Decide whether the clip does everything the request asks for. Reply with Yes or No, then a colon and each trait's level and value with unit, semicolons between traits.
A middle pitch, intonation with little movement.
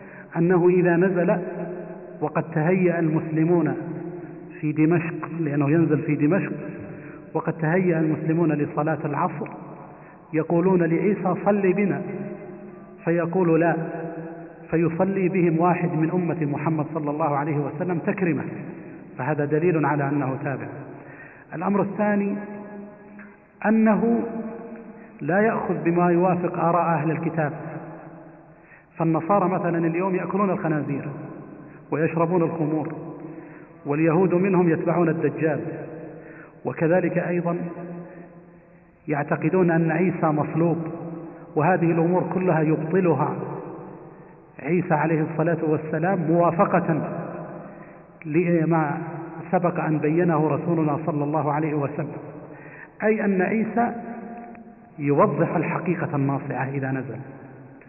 Yes: medium, 165 Hz; narrow, 2.2 semitones